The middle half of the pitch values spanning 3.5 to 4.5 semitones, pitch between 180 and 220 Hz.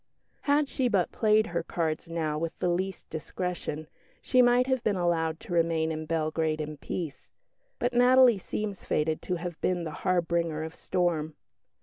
No: average, 4.1 semitones; medium, 170 Hz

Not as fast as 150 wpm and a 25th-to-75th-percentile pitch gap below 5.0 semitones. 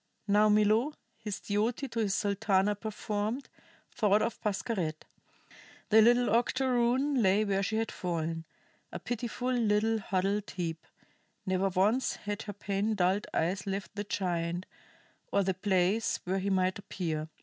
Yes: average, 140 wpm; average, 2.9 semitones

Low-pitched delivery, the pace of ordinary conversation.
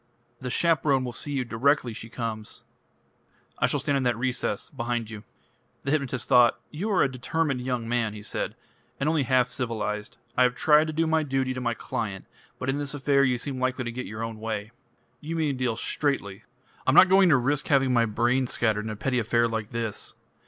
No: low, 125 Hz; fast, 215 wpm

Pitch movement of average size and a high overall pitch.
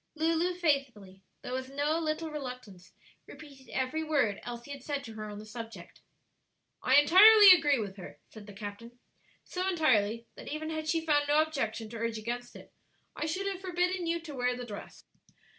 No: wide, 5.8 semitones; very high, 275 Hz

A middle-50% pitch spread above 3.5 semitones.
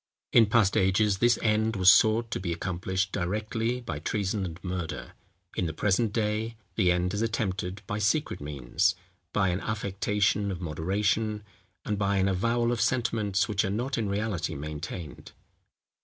No: average, 3.0 semitones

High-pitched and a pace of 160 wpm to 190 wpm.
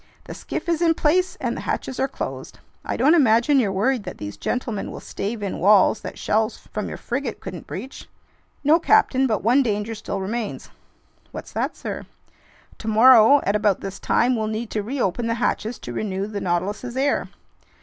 Yes: high, 225 Hz; average, 185 wpm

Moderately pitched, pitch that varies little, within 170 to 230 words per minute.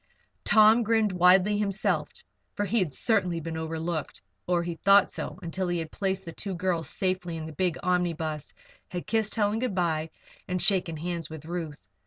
No: medium, 180 Hz; average, 3.2 semitones; average, 180 wpm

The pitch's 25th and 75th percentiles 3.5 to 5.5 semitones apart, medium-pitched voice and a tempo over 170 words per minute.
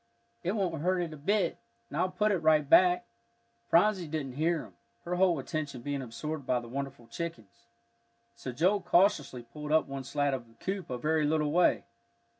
Yes: average, 4.7 semitones; medium, 155 Hz; average, 190 wpm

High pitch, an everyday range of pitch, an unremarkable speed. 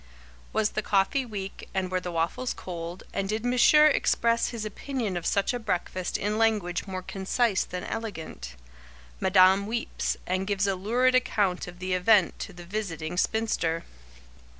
Yes: high, 195 Hz; average, 3.7 semitones; average, 160 wpm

